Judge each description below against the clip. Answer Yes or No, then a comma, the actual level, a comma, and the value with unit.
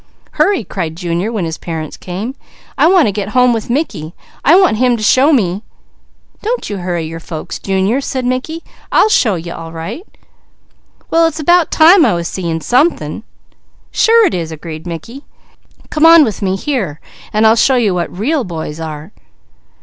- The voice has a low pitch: No, high, 215 Hz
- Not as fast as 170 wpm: No, average, 180 wpm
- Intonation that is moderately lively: No, wide, 8.9 semitones